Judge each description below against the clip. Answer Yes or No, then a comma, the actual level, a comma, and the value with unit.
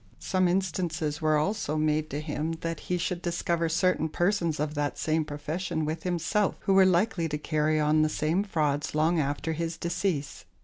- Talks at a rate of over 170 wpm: Yes, average, 180 wpm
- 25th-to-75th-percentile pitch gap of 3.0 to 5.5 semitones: No, narrow, 2.4 semitones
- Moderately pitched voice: Yes, medium, 160 Hz